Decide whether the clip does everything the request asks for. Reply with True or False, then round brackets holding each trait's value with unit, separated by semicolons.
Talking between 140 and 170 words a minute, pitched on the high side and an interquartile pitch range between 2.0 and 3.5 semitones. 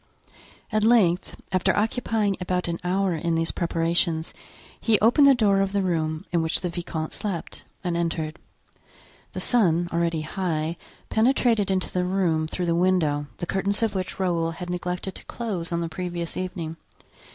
False (165 wpm; 180 Hz; 2.8 semitones)